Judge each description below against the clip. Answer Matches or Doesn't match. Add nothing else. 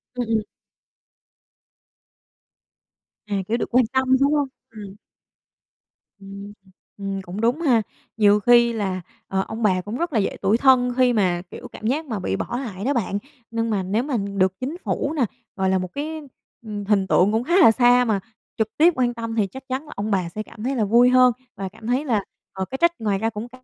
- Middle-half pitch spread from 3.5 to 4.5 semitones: Matches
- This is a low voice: Doesn't match